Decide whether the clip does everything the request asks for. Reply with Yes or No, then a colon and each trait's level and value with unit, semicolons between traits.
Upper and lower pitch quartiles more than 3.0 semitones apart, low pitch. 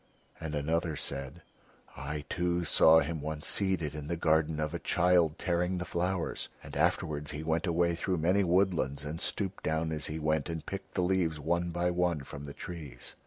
No: narrow, 2.5 semitones; very low, 80 Hz